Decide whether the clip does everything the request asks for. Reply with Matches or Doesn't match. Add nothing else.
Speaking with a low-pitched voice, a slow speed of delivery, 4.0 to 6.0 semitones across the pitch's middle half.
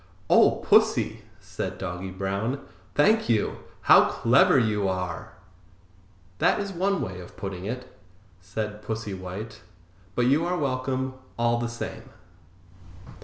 Matches